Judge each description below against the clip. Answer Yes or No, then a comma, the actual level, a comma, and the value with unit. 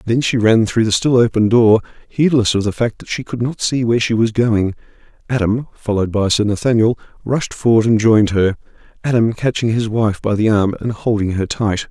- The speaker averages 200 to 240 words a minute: Yes, fast, 205 wpm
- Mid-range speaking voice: No, low, 110 Hz